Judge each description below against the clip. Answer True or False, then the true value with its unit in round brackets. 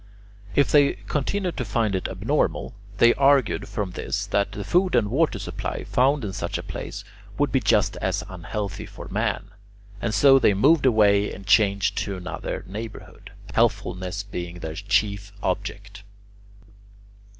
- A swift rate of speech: False (150 wpm)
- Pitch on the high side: False (105 Hz)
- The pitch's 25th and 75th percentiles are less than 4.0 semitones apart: False (4.4 semitones)